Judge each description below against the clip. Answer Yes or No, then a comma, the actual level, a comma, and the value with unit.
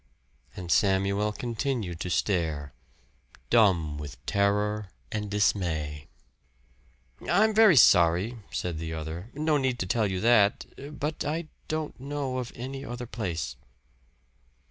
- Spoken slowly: Yes, slow, 120 wpm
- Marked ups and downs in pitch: Yes, wide, 6.7 semitones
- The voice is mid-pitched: No, low, 105 Hz